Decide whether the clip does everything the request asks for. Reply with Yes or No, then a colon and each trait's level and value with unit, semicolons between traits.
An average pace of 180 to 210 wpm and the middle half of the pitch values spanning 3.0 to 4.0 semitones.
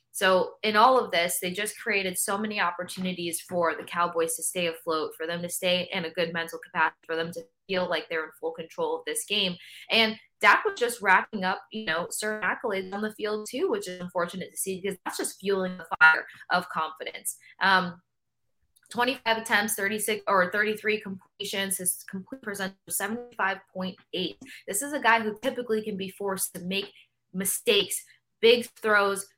Yes: average, 190 wpm; average, 3.5 semitones